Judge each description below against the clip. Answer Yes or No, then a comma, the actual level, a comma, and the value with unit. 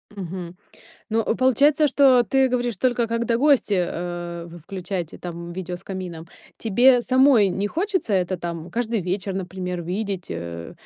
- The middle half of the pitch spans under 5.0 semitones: No, wide, 5.6 semitones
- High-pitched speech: Yes, high, 195 Hz